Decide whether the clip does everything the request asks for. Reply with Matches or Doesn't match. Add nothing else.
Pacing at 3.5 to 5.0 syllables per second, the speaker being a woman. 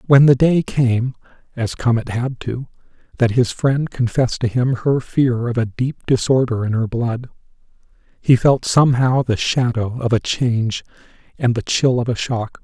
Doesn't match